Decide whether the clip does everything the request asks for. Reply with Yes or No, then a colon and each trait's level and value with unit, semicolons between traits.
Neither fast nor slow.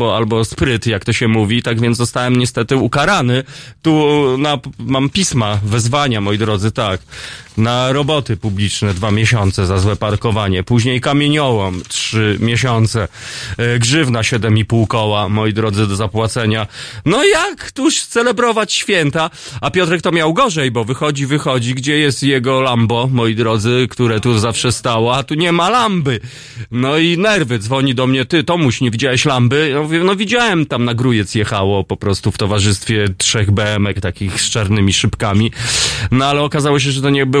No: fast, 170 wpm